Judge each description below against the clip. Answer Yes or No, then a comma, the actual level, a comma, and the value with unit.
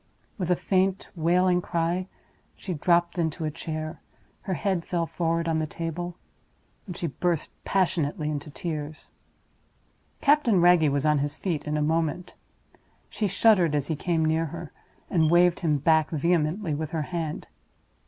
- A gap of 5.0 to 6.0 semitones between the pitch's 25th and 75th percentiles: No, narrow, 2.4 semitones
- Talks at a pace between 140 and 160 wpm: Yes, average, 155 wpm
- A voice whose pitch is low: No, medium, 165 Hz